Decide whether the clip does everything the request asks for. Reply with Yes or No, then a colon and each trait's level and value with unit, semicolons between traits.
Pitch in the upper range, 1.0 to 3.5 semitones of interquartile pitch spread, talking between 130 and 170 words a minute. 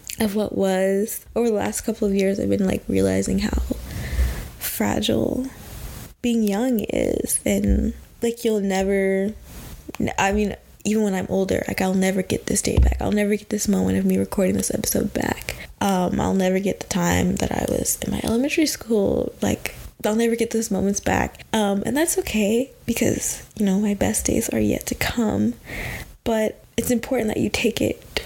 No: high, 210 Hz; average, 3.2 semitones; average, 185 wpm